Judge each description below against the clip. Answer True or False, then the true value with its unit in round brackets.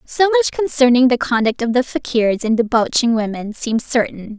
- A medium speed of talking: True (180 wpm)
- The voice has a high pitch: True (245 Hz)